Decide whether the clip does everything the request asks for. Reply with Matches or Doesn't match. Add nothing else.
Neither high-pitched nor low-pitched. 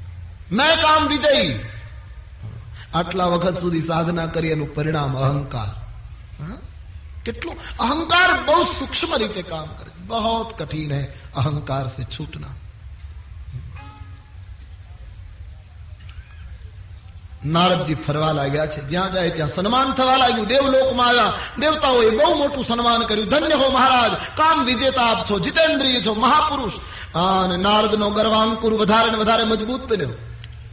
Matches